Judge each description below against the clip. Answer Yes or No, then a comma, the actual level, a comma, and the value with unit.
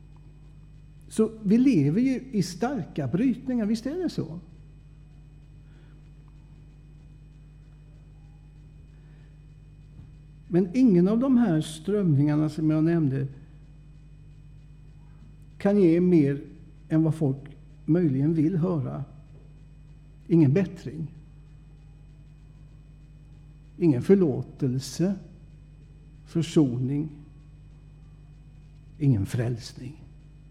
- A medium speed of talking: No, slow, 70 wpm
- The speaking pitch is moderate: Yes, medium, 150 Hz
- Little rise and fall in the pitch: Yes, narrow, 1.2 semitones